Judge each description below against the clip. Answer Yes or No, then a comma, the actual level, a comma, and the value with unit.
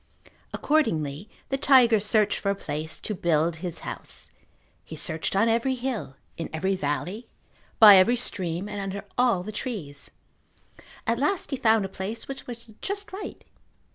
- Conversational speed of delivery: Yes, average, 160 wpm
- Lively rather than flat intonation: Yes, wide, 5.8 semitones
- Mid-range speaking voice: No, high, 210 Hz